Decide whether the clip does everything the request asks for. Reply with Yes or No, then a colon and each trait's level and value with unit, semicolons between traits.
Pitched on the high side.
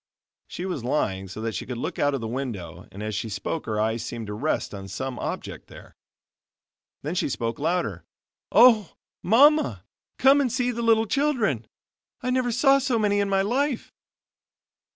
No: medium, 160 Hz